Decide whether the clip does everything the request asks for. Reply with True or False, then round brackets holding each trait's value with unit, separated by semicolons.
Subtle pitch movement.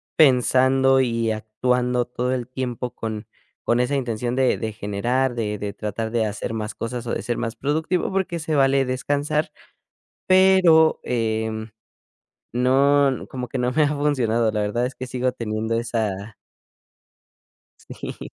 False (3.1 semitones)